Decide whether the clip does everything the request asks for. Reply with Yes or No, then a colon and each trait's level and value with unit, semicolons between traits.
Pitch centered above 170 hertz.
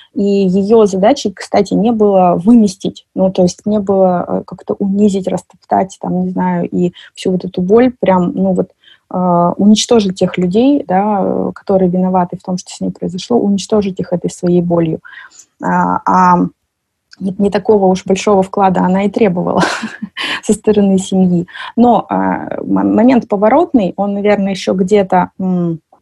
Yes: high, 190 Hz